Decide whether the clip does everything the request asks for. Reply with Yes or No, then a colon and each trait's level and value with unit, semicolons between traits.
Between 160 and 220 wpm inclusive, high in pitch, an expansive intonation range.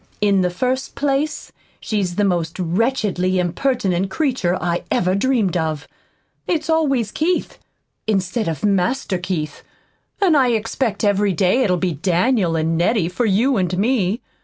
No: average, 145 wpm; high, 195 Hz; wide, 5.9 semitones